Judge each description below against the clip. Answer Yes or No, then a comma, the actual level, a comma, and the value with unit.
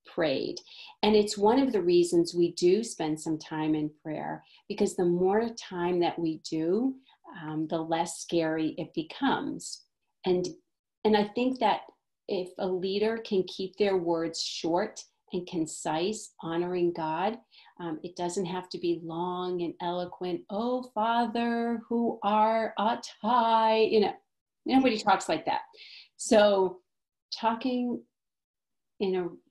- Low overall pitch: No, high, 190 Hz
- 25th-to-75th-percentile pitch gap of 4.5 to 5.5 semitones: Yes, average, 4.8 semitones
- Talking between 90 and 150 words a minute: Yes, average, 140 wpm